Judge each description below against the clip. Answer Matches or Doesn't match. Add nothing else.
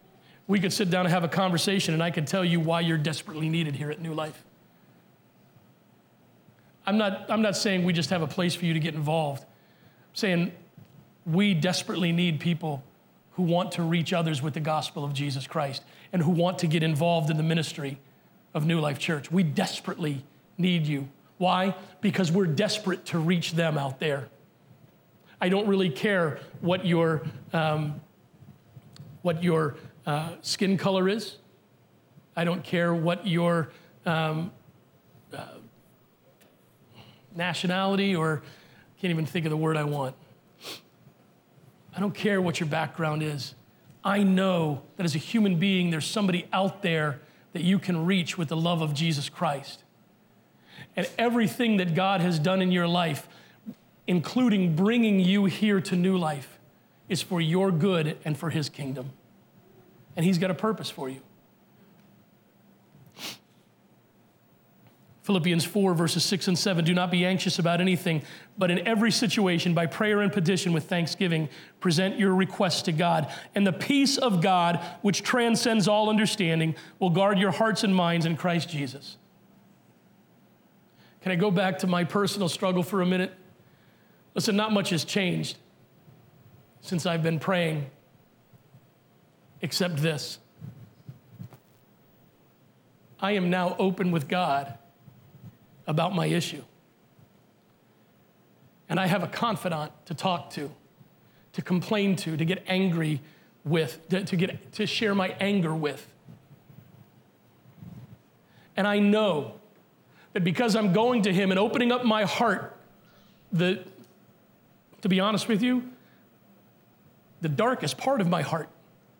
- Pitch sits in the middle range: Matches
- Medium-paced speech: Matches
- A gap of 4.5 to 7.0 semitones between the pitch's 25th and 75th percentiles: Doesn't match